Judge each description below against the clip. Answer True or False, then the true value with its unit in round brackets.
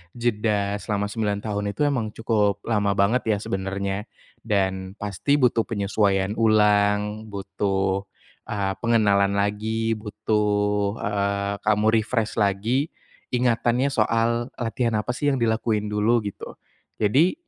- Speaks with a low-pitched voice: True (105 Hz)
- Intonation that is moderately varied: False (2.1 semitones)